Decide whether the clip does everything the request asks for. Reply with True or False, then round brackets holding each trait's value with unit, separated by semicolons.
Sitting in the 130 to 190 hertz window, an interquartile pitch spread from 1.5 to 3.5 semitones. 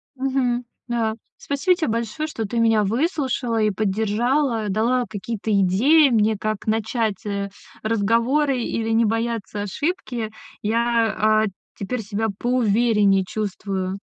False (225 Hz; 2.9 semitones)